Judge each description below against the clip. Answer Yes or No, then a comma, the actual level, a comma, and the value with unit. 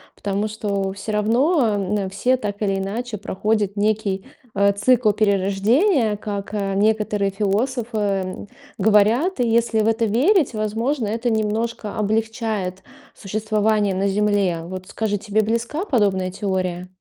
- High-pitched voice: Yes, high, 210 Hz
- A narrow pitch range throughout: Yes, narrow, 2.2 semitones